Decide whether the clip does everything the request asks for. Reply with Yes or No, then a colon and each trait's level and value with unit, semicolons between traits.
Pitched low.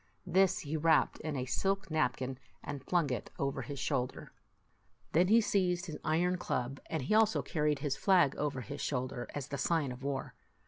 No: medium, 150 Hz